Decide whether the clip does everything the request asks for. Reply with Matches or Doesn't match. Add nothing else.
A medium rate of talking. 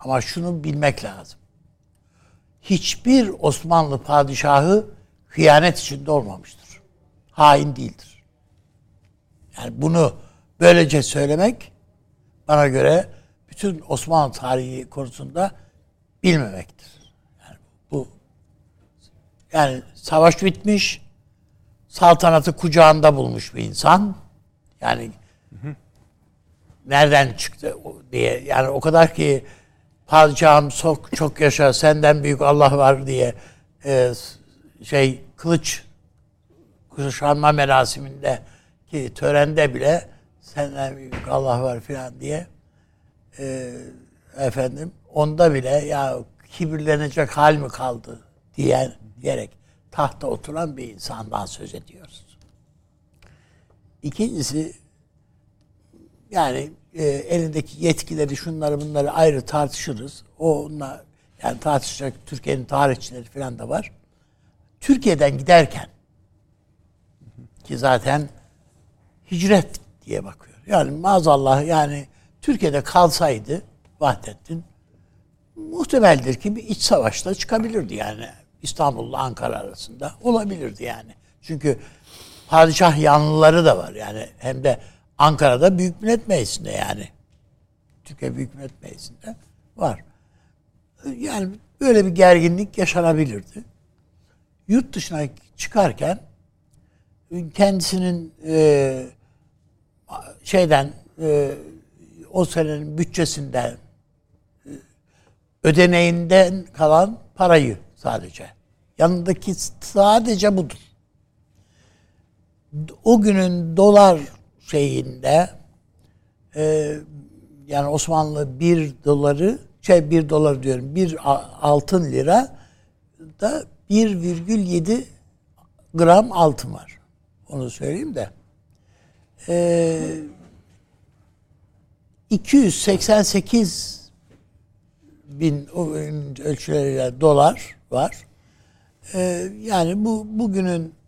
Doesn't match